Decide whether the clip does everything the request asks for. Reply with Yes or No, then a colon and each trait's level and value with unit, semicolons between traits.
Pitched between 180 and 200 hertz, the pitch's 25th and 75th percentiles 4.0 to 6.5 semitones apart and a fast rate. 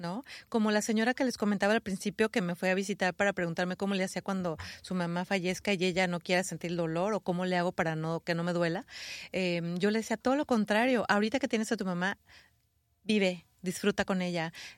No: high, 190 Hz; average, 3.1 semitones; fast, 230 wpm